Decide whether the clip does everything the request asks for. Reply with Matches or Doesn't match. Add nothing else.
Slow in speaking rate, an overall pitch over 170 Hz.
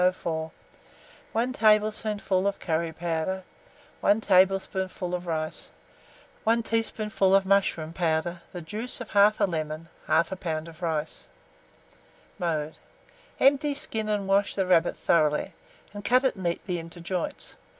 Matches